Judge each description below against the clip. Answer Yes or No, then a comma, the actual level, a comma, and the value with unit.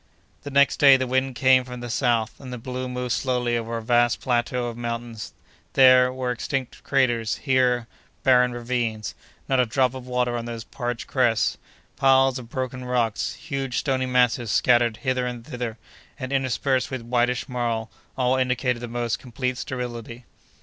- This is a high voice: No, low, 125 Hz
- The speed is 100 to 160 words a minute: No, average, 170 wpm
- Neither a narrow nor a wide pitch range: No, narrow, 1.5 semitones